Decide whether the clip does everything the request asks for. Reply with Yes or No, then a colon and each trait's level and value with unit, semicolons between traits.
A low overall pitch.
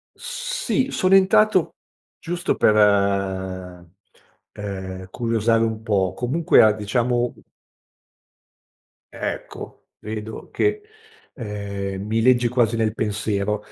Yes: low, 115 Hz